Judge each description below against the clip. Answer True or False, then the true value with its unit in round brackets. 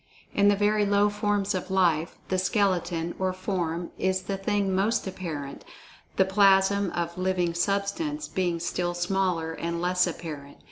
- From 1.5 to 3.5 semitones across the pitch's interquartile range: True (2.5 semitones)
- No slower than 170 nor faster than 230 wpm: False (150 wpm)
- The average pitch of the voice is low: False (185 Hz)